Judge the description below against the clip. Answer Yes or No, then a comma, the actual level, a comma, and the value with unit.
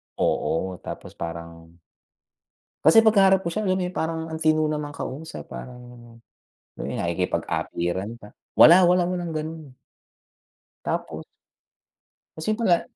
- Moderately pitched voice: Yes, medium, 155 Hz